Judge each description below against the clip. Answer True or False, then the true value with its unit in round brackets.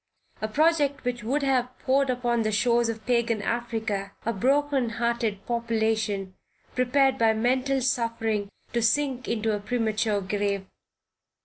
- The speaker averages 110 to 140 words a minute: True (135 wpm)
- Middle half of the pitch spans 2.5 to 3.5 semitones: True (2.8 semitones)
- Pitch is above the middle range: True (235 Hz)